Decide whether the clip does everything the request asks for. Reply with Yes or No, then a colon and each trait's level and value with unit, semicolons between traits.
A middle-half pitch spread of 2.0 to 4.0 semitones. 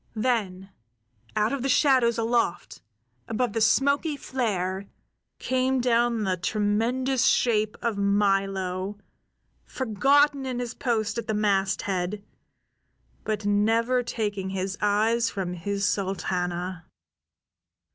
Yes: average, 3.7 semitones